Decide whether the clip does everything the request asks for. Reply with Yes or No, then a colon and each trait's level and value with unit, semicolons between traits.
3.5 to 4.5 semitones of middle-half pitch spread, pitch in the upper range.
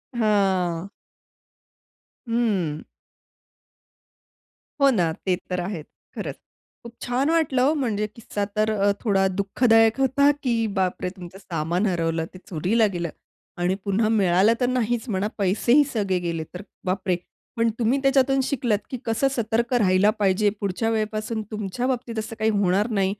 Yes: average, 4.1 semitones; high, 215 Hz